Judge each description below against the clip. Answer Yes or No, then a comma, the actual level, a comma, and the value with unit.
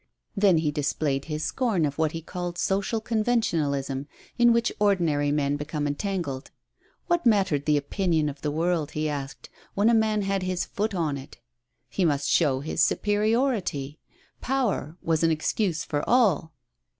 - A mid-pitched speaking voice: Yes, medium, 165 Hz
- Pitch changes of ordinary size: No, wide, 5.8 semitones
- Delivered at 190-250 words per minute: No, average, 165 wpm